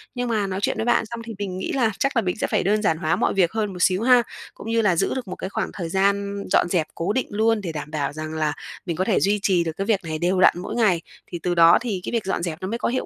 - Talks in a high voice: Yes, high, 195 Hz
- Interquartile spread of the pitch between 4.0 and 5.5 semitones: Yes, average, 4.4 semitones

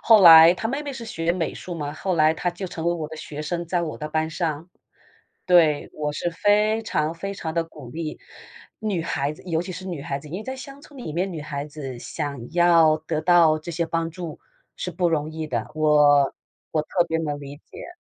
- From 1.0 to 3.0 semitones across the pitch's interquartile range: Yes, narrow, 2.6 semitones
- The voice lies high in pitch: No, medium, 165 Hz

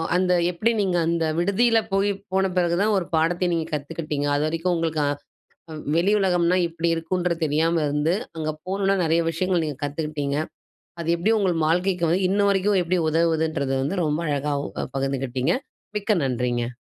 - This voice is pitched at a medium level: Yes, medium, 170 Hz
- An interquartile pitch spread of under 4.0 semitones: Yes, average, 3.5 semitones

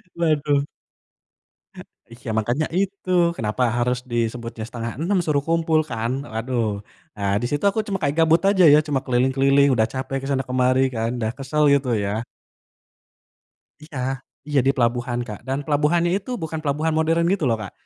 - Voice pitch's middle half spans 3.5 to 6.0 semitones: Yes, average, 4.7 semitones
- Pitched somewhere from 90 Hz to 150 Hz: Yes, low, 135 Hz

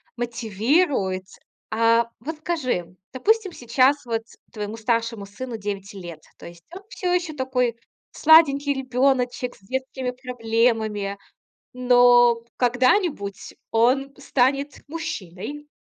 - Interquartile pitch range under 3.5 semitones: No, average, 3.8 semitones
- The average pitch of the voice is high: Yes, high, 245 Hz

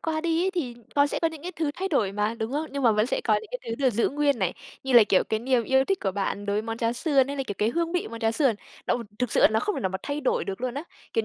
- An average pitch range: No, wide, 5.9 semitones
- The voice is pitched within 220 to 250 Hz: No, very high, 260 Hz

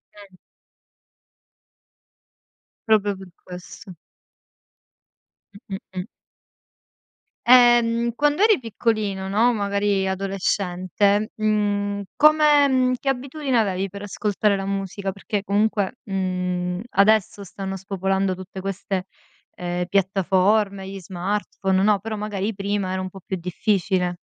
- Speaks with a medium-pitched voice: No, high, 200 Hz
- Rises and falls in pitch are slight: Yes, narrow, 2.2 semitones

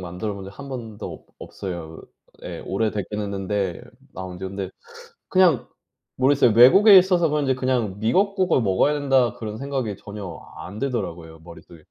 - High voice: No, low, 110 Hz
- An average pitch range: No, wide, 6.2 semitones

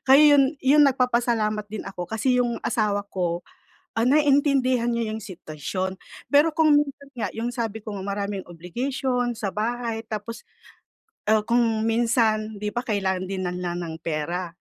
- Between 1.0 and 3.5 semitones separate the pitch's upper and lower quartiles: No, average, 4.1 semitones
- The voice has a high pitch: Yes, high, 225 Hz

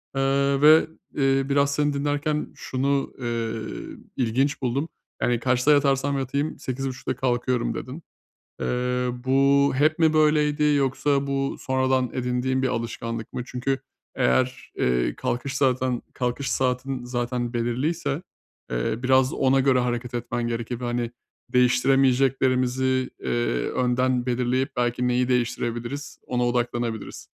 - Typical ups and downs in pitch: No, narrow, 2.0 semitones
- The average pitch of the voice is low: Yes, low, 130 Hz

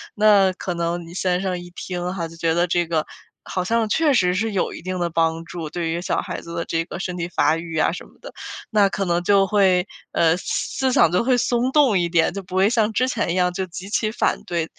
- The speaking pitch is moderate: Yes, medium, 180 Hz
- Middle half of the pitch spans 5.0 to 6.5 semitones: No, average, 2.8 semitones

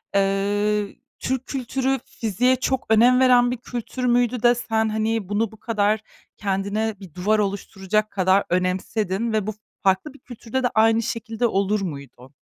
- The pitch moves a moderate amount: Yes, average, 3.4 semitones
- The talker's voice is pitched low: No, high, 220 Hz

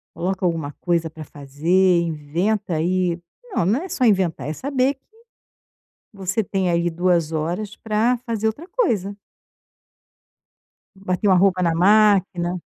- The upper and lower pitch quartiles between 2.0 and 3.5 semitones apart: No, average, 4.0 semitones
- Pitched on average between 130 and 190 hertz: Yes, medium, 185 Hz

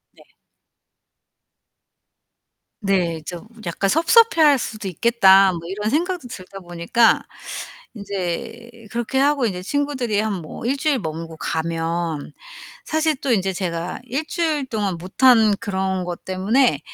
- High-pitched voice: Yes, high, 205 Hz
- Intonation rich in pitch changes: Yes, wide, 6.4 semitones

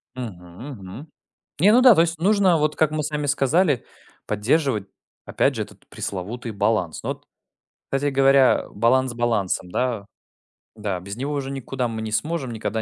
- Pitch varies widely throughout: Yes, wide, 5.9 semitones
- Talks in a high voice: No, low, 130 Hz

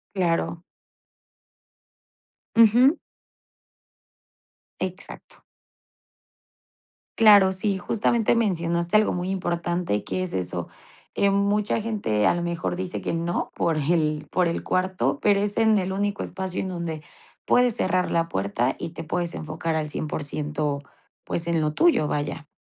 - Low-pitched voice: No, medium, 175 Hz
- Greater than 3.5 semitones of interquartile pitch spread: Yes, average, 4.2 semitones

